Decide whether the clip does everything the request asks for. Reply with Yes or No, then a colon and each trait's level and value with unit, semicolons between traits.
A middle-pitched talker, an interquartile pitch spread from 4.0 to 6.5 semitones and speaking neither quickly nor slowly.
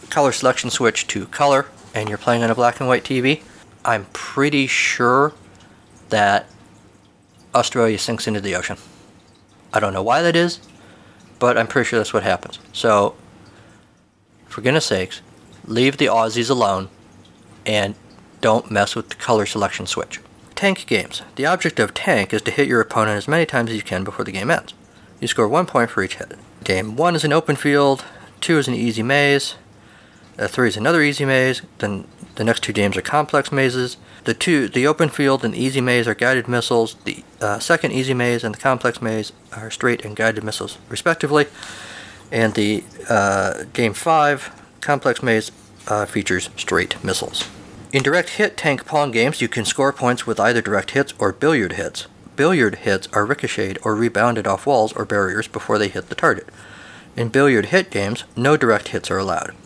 No: low, 120 Hz; average, 4.4 semitones; average, 185 wpm